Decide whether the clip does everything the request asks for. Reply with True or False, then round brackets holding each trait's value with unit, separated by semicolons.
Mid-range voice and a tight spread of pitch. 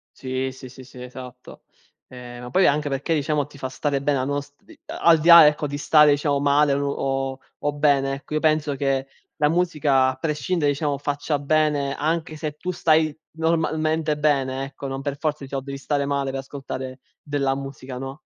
True (145 Hz; 2.1 semitones)